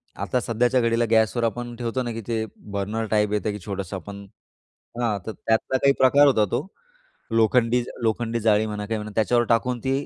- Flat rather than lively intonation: Yes, narrow, 2.3 semitones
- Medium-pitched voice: No, low, 115 Hz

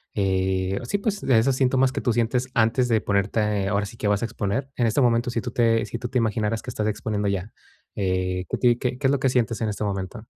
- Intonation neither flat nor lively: Yes, average, 3.4 semitones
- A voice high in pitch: No, low, 115 Hz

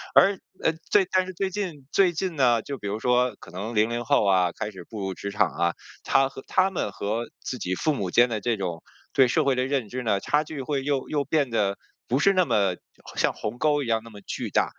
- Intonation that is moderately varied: No, wide, 6.1 semitones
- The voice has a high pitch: No, low, 125 Hz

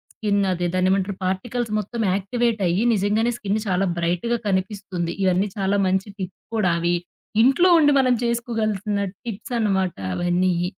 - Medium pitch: No, high, 200 Hz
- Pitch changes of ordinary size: Yes, average, 3.4 semitones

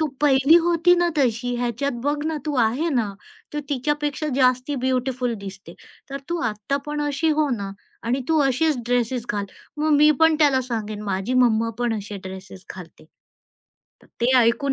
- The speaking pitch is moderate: No, very high, 255 Hz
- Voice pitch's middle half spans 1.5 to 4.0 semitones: No, average, 4.7 semitones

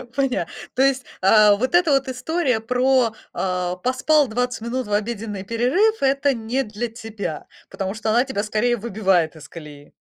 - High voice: Yes, high, 230 Hz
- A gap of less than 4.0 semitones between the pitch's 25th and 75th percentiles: No, average, 4.3 semitones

